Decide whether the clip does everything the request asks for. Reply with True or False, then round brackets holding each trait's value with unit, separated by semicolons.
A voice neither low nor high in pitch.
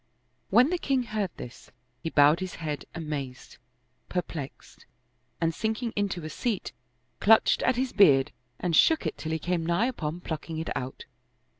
True (170 Hz)